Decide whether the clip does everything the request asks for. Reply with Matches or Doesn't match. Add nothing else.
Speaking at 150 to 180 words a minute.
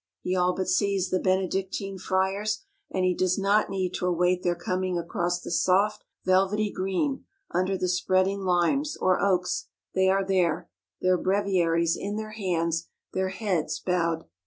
Matches